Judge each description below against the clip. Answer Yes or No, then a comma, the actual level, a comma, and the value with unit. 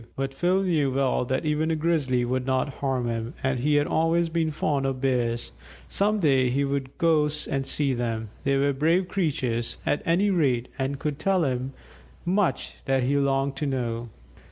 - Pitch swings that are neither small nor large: Yes, average, 3.6 semitones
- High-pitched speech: No, medium, 140 Hz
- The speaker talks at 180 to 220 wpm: Yes, average, 185 wpm